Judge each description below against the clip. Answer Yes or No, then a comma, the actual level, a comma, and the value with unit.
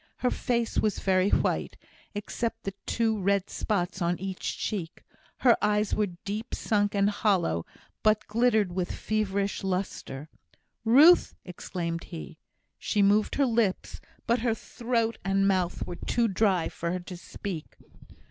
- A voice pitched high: Yes, high, 205 Hz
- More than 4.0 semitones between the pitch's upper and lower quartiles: No, average, 3.3 semitones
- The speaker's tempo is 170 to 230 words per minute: No, average, 140 wpm